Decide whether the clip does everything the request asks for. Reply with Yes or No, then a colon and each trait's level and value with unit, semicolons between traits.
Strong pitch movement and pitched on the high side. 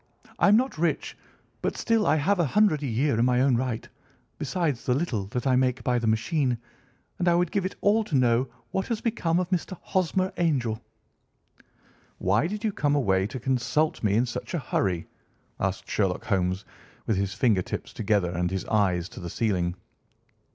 No: wide, 8.3 semitones; low, 125 Hz